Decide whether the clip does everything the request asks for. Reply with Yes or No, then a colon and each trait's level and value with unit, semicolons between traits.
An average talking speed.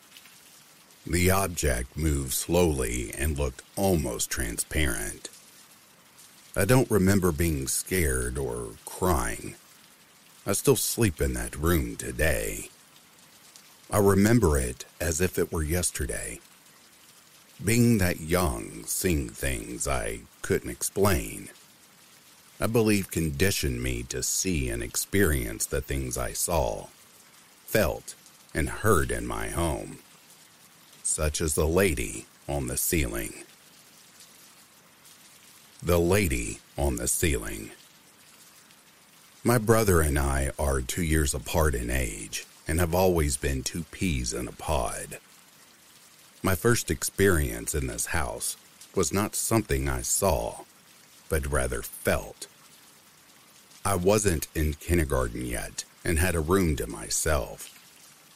No: slow, 115 wpm